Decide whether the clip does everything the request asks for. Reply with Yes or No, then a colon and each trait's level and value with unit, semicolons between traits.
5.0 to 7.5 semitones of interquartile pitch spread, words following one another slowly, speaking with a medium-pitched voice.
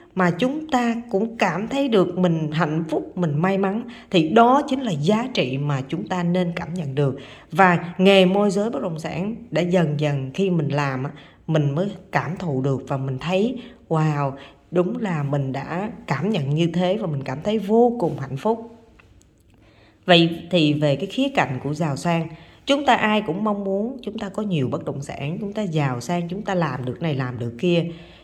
No: wide, 5.6 semitones; average, 210 wpm; medium, 175 Hz